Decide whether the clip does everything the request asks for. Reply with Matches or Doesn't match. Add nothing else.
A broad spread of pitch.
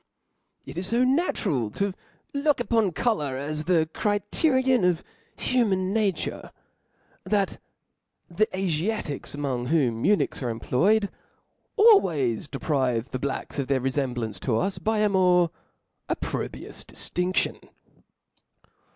Matches